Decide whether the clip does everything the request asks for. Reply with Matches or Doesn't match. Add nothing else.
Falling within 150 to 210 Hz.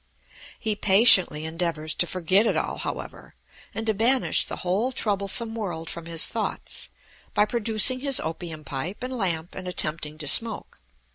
Matches